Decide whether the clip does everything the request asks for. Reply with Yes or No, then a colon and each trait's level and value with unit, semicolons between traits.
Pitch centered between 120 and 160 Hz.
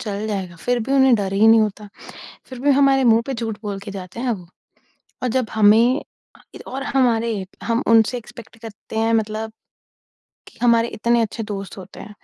No: high, 225 Hz